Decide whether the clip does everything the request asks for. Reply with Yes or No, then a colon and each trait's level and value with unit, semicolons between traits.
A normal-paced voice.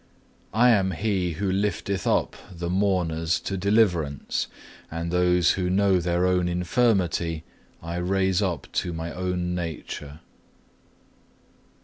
No: slow, 120 wpm